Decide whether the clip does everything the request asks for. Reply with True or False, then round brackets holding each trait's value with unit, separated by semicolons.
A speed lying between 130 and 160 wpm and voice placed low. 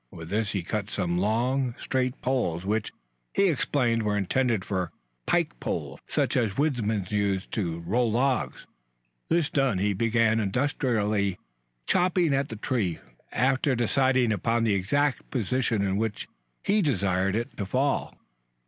True (145 wpm; 115 Hz)